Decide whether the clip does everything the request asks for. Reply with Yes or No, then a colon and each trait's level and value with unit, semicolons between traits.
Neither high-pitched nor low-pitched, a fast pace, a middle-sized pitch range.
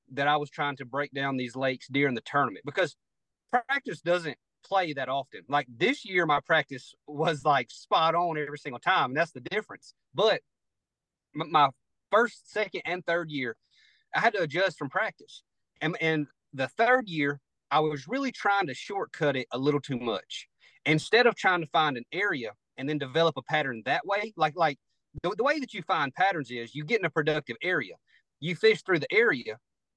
No: medium, 155 Hz; average, 195 wpm; average, 4.5 semitones